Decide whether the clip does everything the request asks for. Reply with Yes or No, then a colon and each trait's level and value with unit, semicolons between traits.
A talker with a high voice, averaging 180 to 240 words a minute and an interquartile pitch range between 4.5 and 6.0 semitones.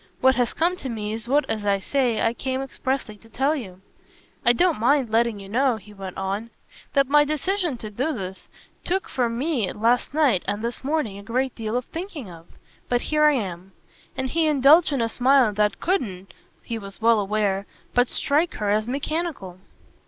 Yes: high, 240 Hz; average, 195 wpm; average, 5.1 semitones